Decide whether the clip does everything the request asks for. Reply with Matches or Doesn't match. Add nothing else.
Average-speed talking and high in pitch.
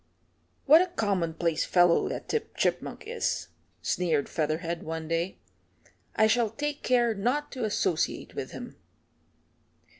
Doesn't match